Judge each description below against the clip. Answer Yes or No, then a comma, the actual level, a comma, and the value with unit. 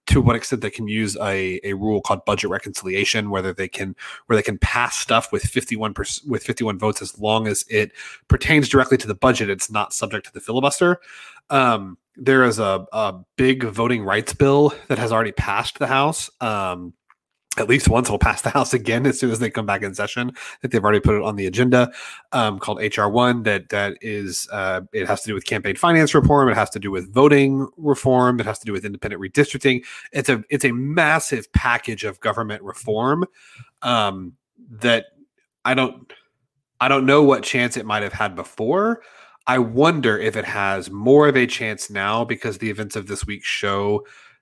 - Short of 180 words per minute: No, fast, 205 wpm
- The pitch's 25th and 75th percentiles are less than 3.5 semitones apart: No, average, 4.5 semitones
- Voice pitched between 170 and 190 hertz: No, low, 115 Hz